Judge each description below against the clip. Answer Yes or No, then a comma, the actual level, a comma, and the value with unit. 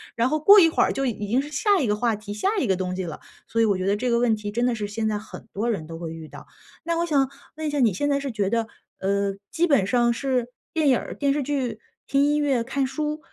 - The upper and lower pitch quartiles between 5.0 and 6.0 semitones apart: Yes, wide, 5.4 semitones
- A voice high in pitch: Yes, high, 240 Hz